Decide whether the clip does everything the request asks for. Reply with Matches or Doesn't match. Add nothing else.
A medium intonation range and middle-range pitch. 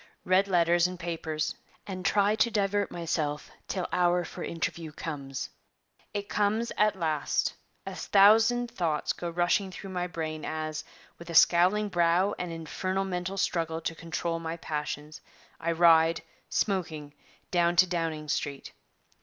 Matches